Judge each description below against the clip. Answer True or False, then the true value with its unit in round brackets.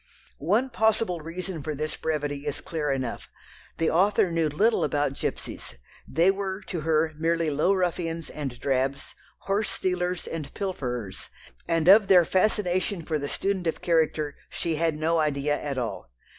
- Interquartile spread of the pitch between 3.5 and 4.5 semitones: True (3.8 semitones)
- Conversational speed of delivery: True (155 wpm)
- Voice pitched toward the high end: False (165 Hz)